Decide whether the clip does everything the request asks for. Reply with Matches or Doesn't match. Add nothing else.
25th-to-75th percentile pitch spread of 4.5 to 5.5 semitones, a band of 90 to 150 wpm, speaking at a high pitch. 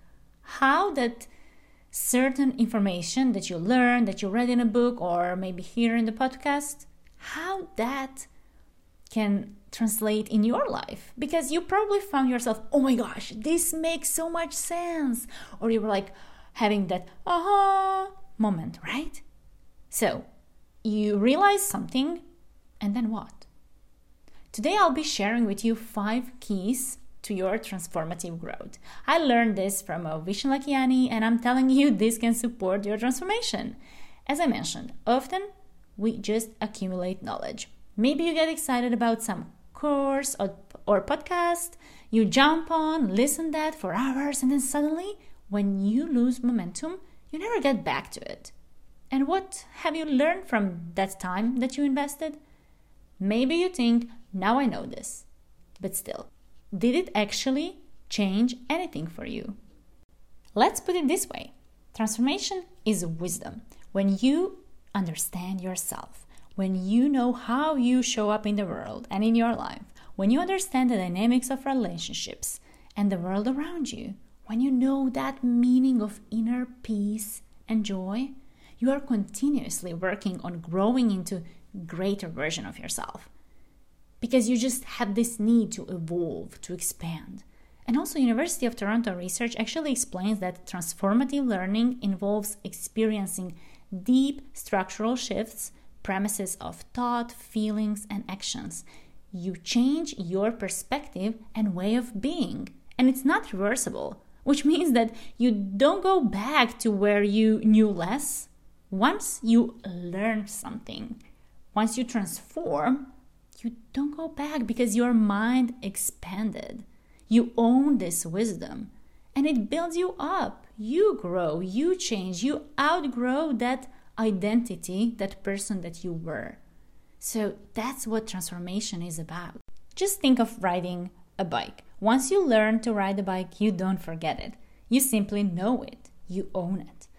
Matches